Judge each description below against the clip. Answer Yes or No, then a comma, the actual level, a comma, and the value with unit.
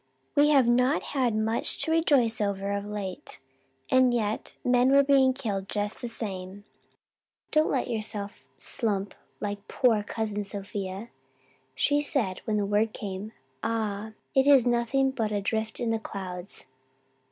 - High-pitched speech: Yes, high, 220 Hz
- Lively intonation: No, average, 3.8 semitones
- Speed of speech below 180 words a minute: Yes, average, 150 wpm